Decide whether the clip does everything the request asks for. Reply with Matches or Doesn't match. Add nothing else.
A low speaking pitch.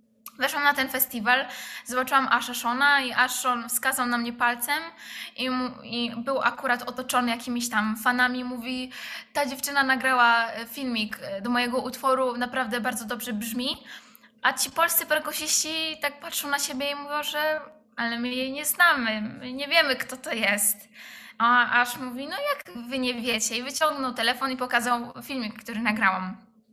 Doesn't match